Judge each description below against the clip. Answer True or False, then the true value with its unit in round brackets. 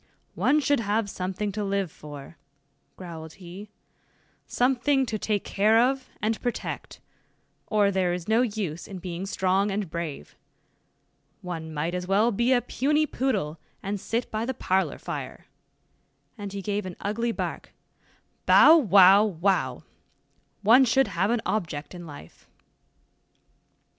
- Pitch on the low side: False (200 Hz)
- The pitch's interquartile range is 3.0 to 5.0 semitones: True (4.2 semitones)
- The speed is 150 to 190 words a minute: False (140 wpm)